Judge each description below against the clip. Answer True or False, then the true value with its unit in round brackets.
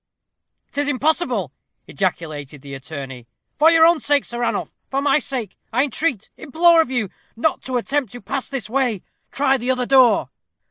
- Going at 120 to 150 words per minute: False (170 wpm)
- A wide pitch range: True (6.2 semitones)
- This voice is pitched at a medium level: False (255 Hz)